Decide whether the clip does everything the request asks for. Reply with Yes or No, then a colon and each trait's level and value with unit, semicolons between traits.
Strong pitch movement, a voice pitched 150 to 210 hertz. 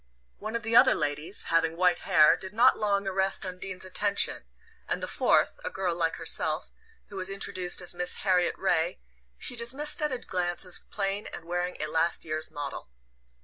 No: average, 2.7 semitones; medium, 185 Hz